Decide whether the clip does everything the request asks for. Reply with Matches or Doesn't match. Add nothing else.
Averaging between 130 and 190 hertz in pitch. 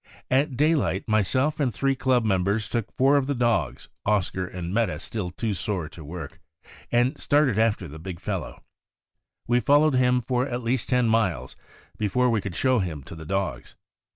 Doesn't match